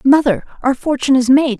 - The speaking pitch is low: No, very high, 265 Hz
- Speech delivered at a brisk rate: No, average, 190 wpm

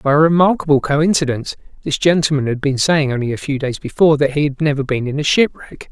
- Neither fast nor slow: No, fast, 225 wpm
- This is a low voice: No, medium, 145 Hz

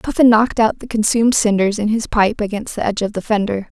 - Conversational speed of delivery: No, fast, 235 wpm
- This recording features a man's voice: No, female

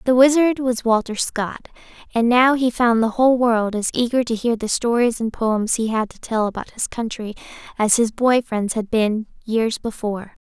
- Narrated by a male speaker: No, female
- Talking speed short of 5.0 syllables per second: Yes, 4.8 syllables/s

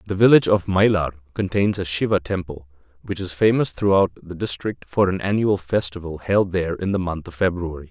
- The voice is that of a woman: No, male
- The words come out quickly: No, average, 190 wpm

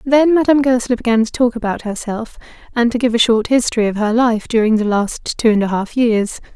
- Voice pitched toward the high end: Yes, high, 230 Hz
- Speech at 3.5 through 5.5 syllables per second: No, 5.7 syllables/s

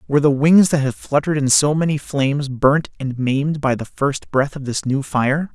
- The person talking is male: Yes, male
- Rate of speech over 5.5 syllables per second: No, 5.1 syllables/s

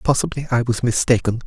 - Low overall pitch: Yes, low, 125 Hz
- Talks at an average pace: Yes, average, 165 wpm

